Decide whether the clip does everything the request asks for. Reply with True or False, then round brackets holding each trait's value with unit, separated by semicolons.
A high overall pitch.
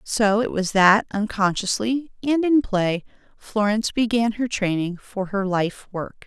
True (210 Hz)